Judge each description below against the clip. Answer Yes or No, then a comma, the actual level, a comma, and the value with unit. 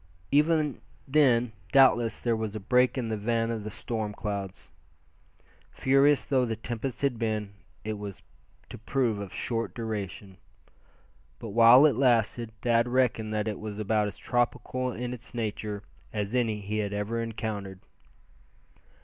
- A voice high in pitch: No, low, 115 Hz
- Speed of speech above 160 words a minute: No, average, 150 wpm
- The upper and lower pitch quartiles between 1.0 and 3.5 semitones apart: Yes, average, 2.8 semitones